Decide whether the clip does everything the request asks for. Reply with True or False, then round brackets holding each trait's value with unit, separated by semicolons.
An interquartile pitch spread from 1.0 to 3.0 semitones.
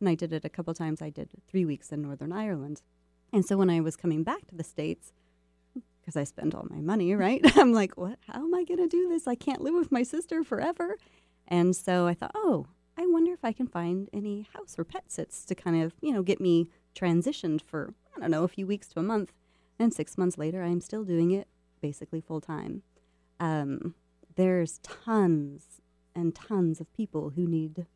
False (5.1 semitones)